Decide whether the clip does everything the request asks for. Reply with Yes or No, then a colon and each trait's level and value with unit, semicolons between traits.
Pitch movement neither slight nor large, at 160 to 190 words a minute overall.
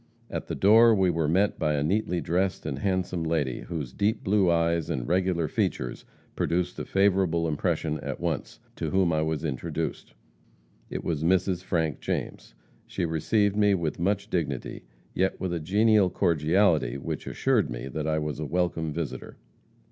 Yes: average, 3.5 semitones; average, 170 wpm